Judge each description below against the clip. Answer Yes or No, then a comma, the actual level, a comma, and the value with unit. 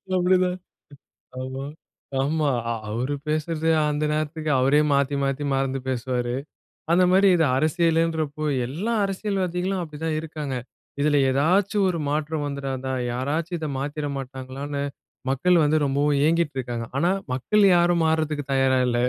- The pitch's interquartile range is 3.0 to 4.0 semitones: Yes, average, 3.7 semitones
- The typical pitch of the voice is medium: Yes, medium, 150 Hz